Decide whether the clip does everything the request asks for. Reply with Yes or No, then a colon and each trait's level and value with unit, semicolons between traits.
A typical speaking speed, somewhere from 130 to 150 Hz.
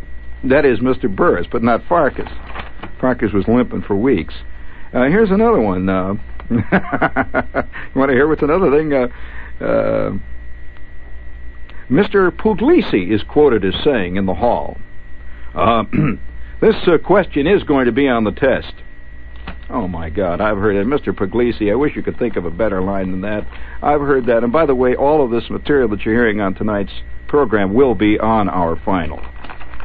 No: average, 175 wpm; very low, 95 Hz